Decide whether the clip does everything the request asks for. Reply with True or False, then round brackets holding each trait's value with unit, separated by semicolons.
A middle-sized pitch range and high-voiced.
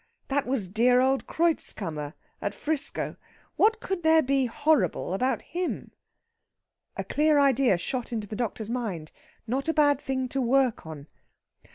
True (4.9 semitones; 260 Hz)